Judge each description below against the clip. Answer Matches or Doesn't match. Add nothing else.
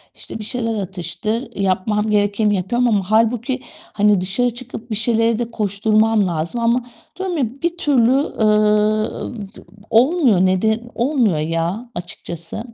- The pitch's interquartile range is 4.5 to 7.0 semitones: Doesn't match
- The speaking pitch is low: Doesn't match